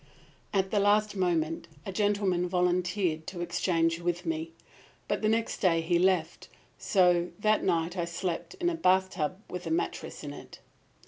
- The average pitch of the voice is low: No, medium, 180 Hz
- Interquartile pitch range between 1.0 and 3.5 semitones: Yes, narrow, 2.4 semitones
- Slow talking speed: No, average, 160 wpm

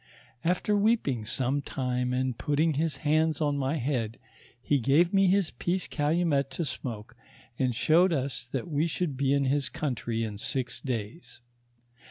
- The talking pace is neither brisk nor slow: Yes, average, 160 wpm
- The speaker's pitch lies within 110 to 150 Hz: Yes, medium, 140 Hz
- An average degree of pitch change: Yes, average, 4.4 semitones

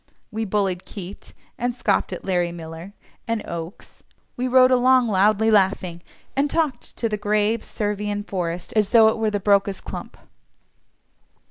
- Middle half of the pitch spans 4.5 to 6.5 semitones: No, average, 3.3 semitones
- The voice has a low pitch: No, high, 210 Hz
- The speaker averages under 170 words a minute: Yes, average, 150 wpm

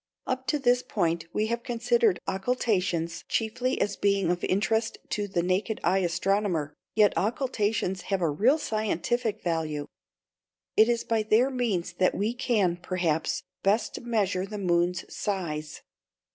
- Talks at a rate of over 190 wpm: No, average, 145 wpm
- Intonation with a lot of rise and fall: No, average, 4.6 semitones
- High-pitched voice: Yes, high, 200 Hz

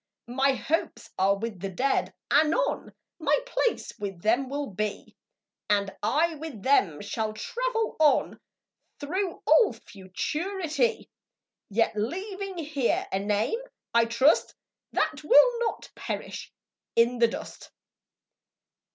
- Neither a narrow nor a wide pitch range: No, wide, 8.4 semitones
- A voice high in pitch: Yes, very high, 275 Hz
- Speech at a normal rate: No, slow, 115 wpm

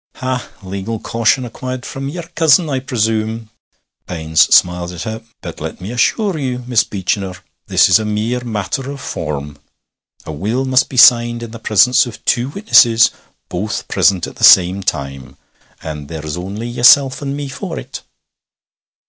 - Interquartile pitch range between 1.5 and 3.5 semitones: No, wide, 5.6 semitones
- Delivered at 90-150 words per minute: No, average, 165 wpm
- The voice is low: Yes, low, 115 Hz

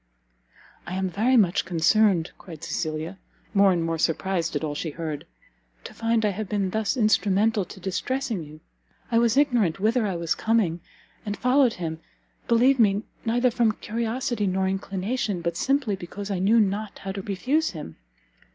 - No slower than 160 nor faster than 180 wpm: Yes, average, 170 wpm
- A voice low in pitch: No, high, 200 Hz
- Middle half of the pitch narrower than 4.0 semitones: No, average, 4.3 semitones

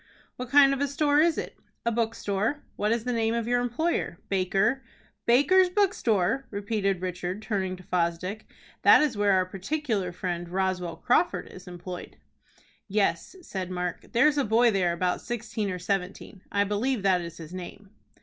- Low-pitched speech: No, high, 205 Hz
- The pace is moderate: Yes, average, 170 wpm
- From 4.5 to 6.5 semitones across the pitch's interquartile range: Yes, average, 5.0 semitones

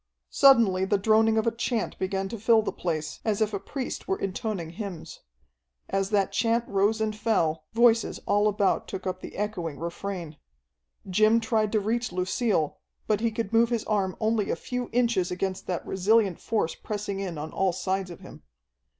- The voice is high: Yes, high, 205 Hz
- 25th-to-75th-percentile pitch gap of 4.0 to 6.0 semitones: No, average, 3.1 semitones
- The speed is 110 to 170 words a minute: No, average, 185 wpm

